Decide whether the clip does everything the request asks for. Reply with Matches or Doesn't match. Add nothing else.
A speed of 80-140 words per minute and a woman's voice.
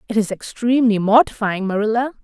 Matches